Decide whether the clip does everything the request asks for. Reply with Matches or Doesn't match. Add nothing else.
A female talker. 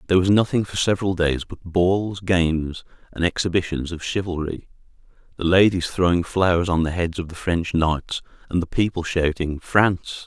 Doesn't match